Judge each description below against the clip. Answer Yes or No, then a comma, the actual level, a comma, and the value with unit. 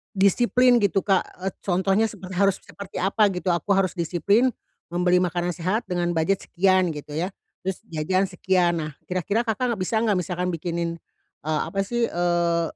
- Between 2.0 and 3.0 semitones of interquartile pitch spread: Yes, narrow, 2.4 semitones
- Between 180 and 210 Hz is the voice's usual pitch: Yes, medium, 185 Hz